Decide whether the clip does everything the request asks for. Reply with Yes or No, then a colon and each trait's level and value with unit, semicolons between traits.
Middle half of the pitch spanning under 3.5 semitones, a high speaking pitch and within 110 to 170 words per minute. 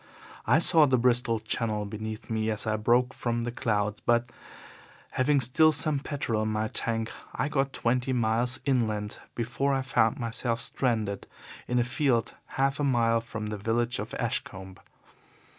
No: average, 2.9 semitones; low, 120 Hz; average, 160 wpm